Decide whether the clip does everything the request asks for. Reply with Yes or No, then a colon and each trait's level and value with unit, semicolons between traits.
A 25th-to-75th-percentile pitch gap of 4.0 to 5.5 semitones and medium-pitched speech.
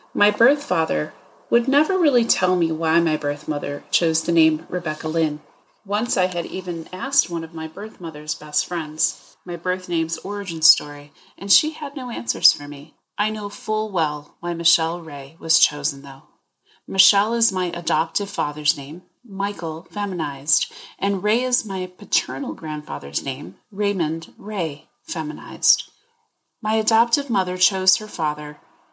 Yes: average, 4.6 semitones; medium, 175 Hz